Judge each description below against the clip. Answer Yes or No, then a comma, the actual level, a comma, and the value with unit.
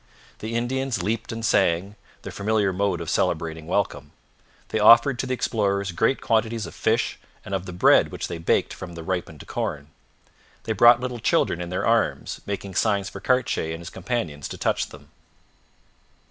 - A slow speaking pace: No, average, 175 wpm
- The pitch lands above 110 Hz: No, low, 100 Hz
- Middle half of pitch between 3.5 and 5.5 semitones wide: Yes, average, 4.8 semitones